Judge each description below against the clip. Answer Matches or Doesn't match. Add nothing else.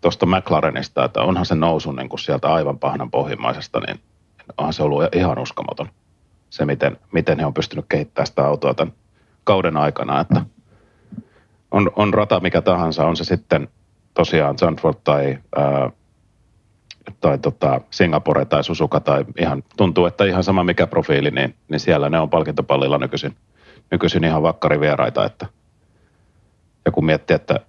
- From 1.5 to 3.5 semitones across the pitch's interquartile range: Doesn't match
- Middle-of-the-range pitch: Doesn't match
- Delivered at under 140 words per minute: Doesn't match